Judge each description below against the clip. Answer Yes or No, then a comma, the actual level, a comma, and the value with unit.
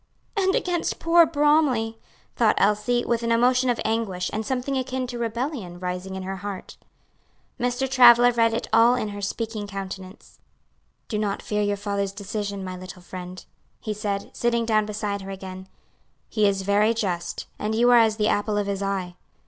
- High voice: Yes, high, 215 Hz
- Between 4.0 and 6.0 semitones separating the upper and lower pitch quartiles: No, average, 3.4 semitones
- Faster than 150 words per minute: Yes, average, 180 wpm